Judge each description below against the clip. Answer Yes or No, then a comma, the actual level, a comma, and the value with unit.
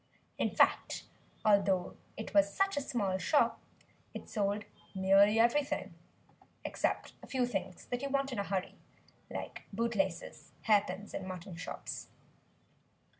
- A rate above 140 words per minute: No, slow, 135 wpm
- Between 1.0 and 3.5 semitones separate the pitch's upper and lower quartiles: No, average, 4.1 semitones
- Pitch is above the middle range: Yes, high, 205 Hz